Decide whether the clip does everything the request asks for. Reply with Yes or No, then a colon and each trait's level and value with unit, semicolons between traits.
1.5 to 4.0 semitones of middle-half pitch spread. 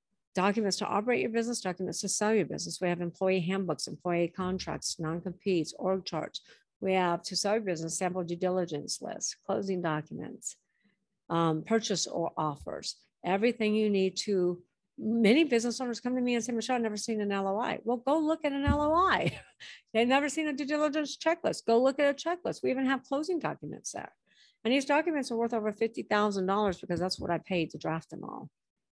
No: average, 5.0 semitones